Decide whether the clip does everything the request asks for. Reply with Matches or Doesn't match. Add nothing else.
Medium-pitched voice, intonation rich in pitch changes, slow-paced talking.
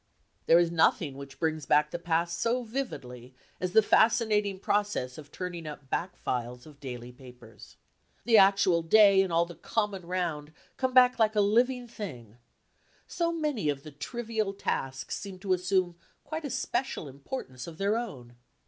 Doesn't match